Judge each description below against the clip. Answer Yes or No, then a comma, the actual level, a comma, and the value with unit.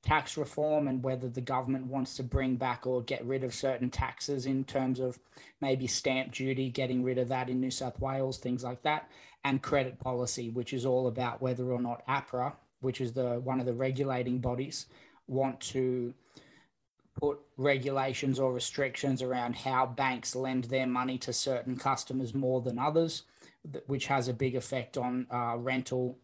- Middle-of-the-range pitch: No, low, 130 Hz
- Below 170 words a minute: No, average, 180 wpm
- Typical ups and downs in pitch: No, narrow, 1.1 semitones